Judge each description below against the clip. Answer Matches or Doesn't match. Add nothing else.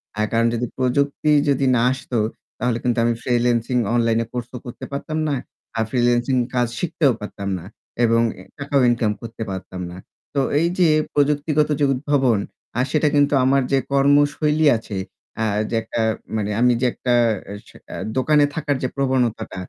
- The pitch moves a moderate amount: Matches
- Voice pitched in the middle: Doesn't match